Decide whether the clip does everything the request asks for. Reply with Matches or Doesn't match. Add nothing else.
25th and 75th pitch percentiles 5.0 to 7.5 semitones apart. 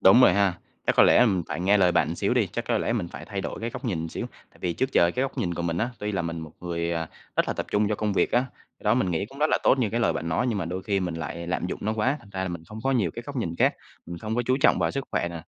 Matches